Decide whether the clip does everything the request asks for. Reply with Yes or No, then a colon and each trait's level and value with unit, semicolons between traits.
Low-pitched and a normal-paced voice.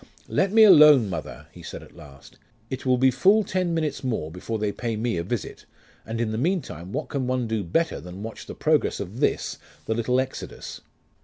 No: low, 115 Hz; fast, 210 wpm